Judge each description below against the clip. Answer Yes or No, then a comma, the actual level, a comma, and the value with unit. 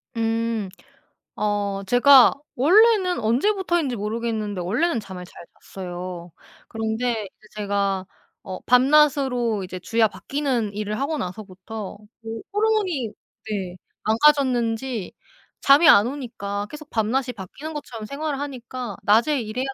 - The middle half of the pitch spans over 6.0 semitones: No, average, 5.3 semitones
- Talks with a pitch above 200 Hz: Yes, high, 230 Hz